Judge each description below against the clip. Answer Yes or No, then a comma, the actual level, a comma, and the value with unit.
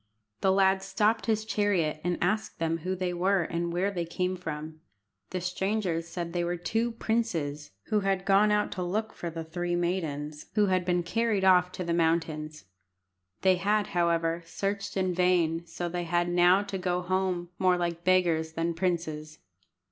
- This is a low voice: No, medium, 180 Hz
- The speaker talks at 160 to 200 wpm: Yes, average, 180 wpm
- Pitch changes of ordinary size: No, narrow, 2.3 semitones